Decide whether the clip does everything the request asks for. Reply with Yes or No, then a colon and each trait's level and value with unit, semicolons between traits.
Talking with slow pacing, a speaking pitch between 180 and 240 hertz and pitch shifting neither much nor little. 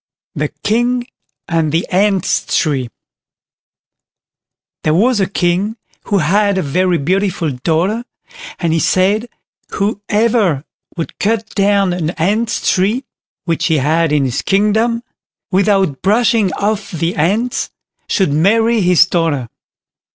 Yes: slow, 120 wpm; high, 190 Hz; average, 4.4 semitones